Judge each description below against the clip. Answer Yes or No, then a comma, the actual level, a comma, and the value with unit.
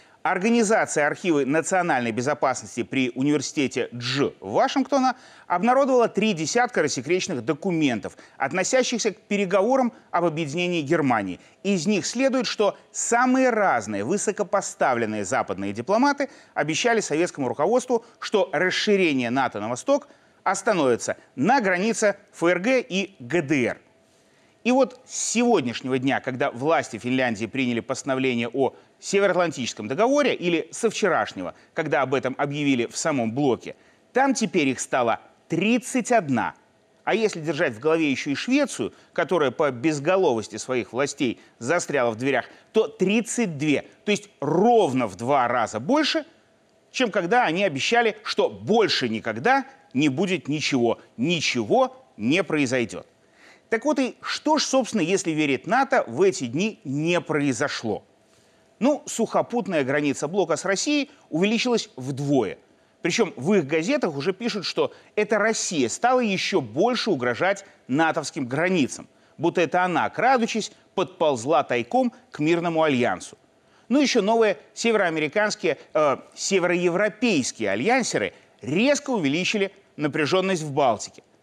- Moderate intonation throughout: No, wide, 8.2 semitones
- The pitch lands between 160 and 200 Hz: Yes, high, 190 Hz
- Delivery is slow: No, average, 120 wpm